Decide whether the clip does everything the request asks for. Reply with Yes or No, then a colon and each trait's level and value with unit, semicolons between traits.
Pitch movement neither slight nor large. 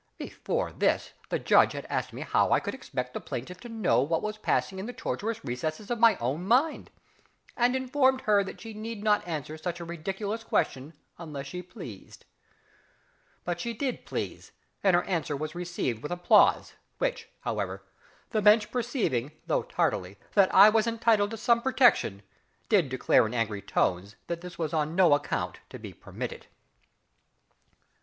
No: wide, 6.8 semitones